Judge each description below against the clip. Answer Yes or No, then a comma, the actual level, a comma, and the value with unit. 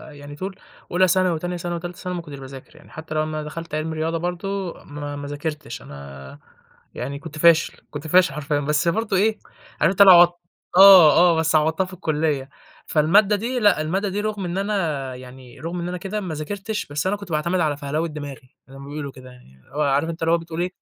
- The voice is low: No, medium, 160 Hz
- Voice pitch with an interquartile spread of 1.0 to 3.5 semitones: No, average, 3.9 semitones